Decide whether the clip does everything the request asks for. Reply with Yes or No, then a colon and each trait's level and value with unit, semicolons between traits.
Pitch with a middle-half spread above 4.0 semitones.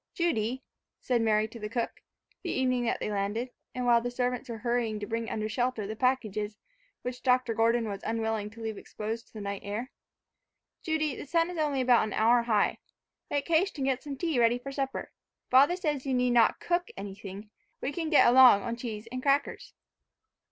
No: average, 3.3 semitones